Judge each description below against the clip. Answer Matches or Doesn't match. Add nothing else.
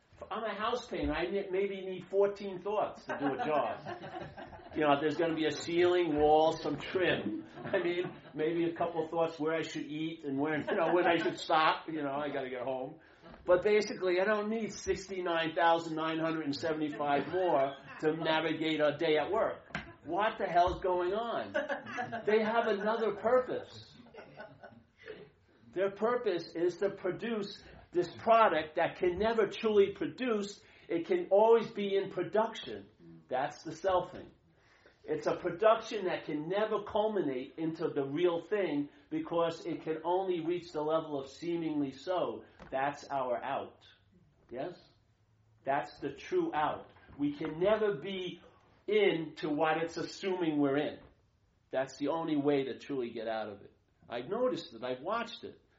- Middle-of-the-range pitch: Matches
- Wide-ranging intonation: Doesn't match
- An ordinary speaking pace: Matches